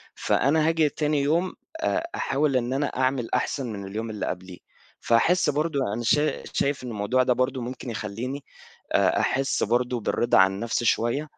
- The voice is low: Yes, low, 130 Hz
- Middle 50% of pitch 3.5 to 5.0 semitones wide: Yes, average, 3.9 semitones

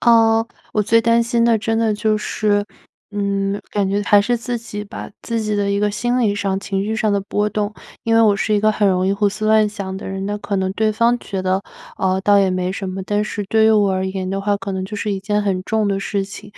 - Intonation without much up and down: Yes, narrow, 1.8 semitones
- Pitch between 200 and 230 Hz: Yes, high, 205 Hz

